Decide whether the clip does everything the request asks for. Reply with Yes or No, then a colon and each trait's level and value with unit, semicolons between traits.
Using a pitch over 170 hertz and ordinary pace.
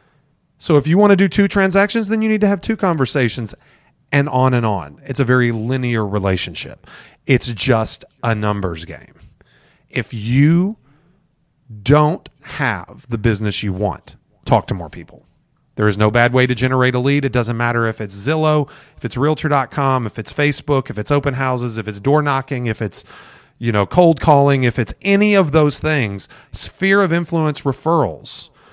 No: low, 135 Hz; average, 180 wpm